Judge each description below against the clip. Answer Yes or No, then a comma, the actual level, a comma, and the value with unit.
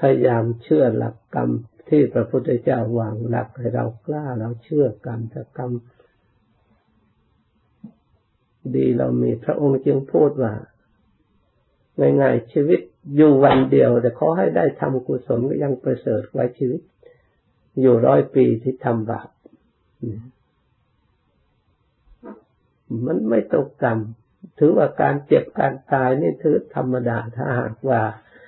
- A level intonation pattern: No, average, 3.1 semitones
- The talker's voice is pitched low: Yes, low, 120 Hz